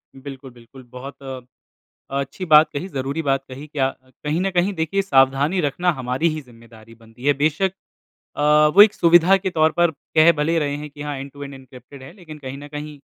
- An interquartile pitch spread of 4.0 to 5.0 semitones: No, average, 3.3 semitones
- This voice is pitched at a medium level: Yes, medium, 145 Hz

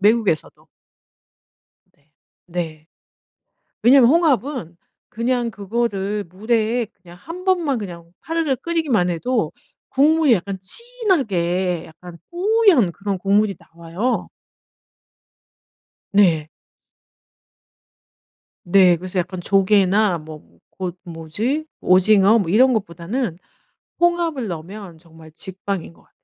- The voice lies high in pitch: Yes, high, 200 Hz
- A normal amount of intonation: No, wide, 6.5 semitones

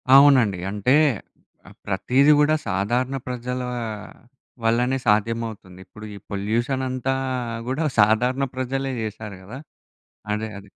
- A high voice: No, low, 120 Hz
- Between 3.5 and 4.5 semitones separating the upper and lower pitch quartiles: Yes, average, 3.9 semitones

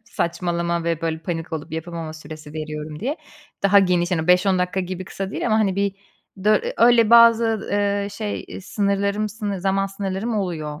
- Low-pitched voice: No, high, 190 Hz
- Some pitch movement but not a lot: Yes, average, 3.5 semitones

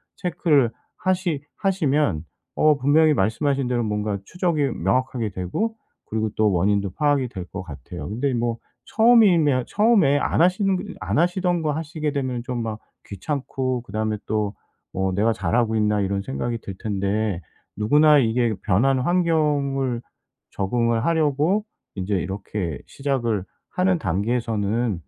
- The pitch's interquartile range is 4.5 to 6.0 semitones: No, wide, 6.4 semitones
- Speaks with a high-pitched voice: No, low, 125 Hz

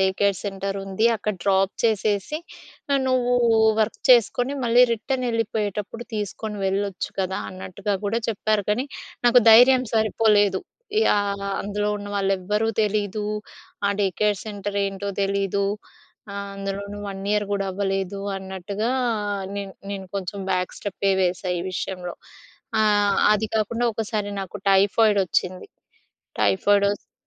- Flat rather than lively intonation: Yes, narrow, 1.7 semitones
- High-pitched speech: Yes, high, 200 Hz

